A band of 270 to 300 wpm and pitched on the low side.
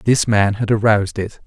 No: fast, 205 wpm; low, 105 Hz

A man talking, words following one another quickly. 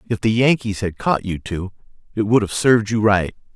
Yes: male; fast, 220 wpm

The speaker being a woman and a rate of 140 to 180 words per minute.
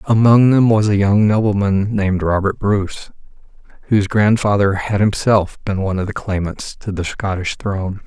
No: male; average, 165 wpm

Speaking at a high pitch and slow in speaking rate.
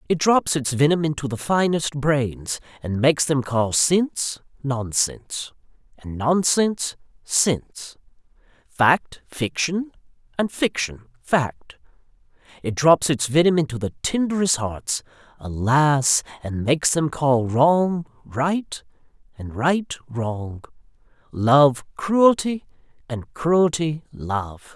No: medium, 145 Hz; slow, 110 wpm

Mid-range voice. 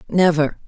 Yes: medium, 165 Hz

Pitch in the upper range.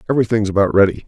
No: low, 105 Hz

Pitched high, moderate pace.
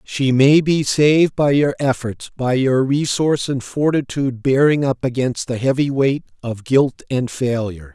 No: low, 135 Hz; average, 165 wpm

